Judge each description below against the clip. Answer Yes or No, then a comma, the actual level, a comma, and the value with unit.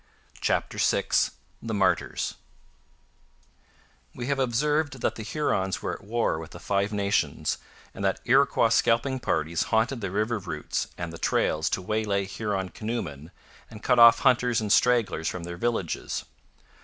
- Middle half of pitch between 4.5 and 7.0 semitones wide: No, average, 4.0 semitones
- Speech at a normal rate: Yes, average, 150 wpm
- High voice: No, low, 110 Hz